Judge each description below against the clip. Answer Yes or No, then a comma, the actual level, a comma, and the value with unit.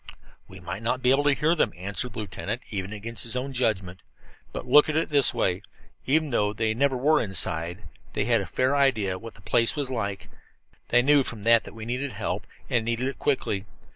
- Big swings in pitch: No, average, 4.6 semitones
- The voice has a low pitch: Yes, low, 115 Hz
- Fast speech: Yes, fast, 225 wpm